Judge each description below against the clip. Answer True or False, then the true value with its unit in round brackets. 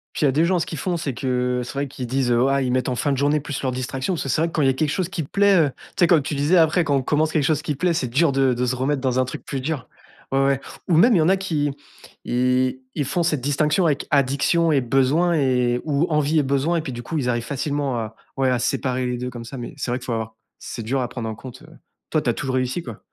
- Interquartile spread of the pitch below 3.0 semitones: False (3.5 semitones)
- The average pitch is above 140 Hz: False (135 Hz)